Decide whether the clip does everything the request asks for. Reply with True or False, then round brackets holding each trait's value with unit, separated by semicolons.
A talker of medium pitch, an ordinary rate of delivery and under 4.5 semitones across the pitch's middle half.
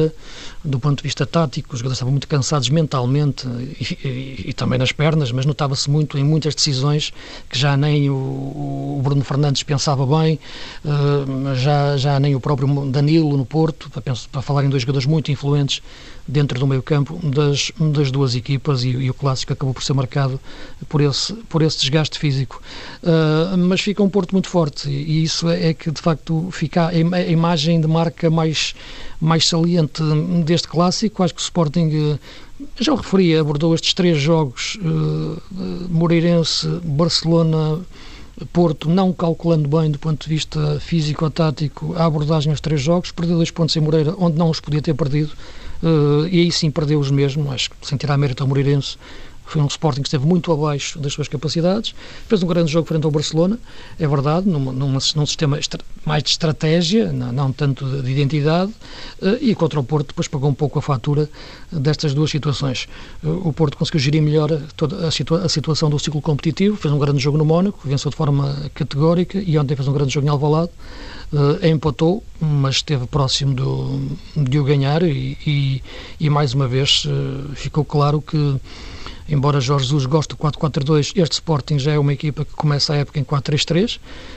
False (150 Hz; 190 wpm; 2.5 semitones)